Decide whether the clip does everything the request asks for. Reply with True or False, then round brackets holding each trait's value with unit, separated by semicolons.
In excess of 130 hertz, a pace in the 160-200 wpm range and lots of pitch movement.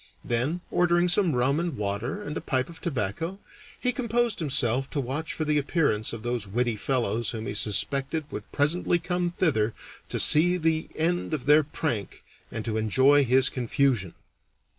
True (140 Hz; 170 wpm; 6.0 semitones)